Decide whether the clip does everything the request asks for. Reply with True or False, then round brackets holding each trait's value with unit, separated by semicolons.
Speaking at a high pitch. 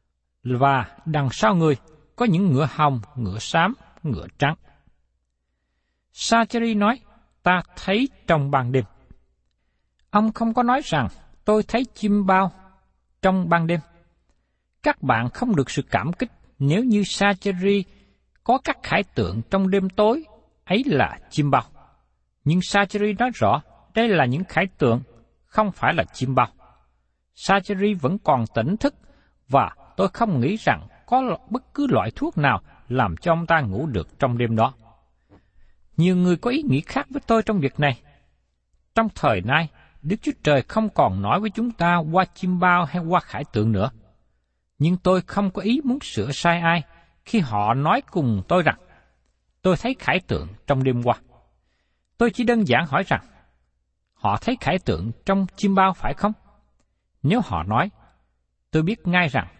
False (160 Hz)